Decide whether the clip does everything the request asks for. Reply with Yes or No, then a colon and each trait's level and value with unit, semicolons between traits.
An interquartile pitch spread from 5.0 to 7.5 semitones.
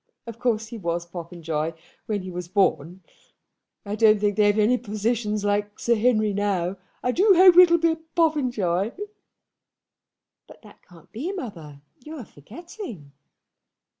Yes: wide, 5.5 semitones